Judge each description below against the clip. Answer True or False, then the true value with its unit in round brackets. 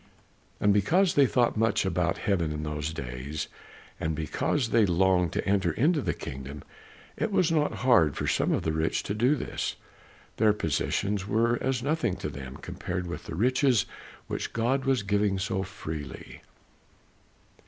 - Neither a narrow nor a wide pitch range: False (7.2 semitones)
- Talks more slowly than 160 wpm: False (165 wpm)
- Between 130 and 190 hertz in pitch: False (100 Hz)